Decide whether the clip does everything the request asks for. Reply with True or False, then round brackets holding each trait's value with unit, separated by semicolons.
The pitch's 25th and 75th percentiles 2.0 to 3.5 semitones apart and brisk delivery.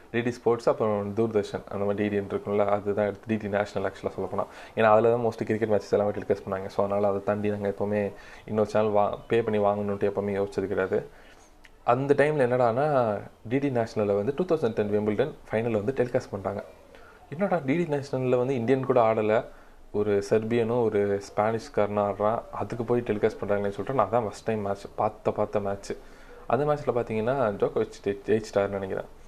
True (2.8 semitones; 170 wpm)